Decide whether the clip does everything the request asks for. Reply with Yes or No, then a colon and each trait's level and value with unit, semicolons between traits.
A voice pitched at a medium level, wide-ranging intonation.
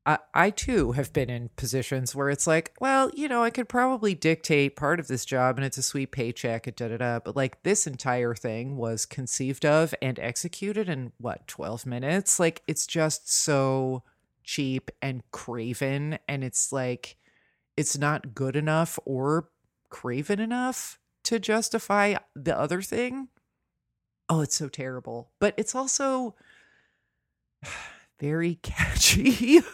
Yes: medium, 145 Hz; wide, 7.0 semitones